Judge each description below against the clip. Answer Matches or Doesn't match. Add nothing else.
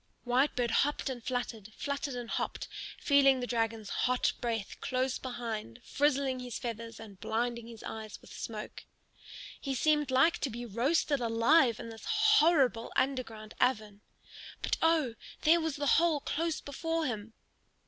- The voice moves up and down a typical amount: Matches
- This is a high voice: Matches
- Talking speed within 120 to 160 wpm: Matches